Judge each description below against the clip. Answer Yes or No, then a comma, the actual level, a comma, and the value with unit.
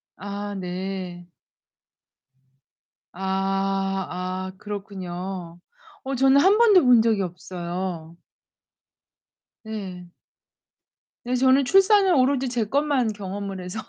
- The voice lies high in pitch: Yes, high, 195 Hz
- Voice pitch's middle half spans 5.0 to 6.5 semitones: Yes, wide, 5.4 semitones